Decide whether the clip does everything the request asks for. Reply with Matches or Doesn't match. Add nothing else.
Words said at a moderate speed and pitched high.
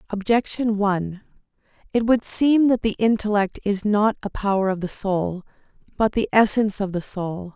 Matches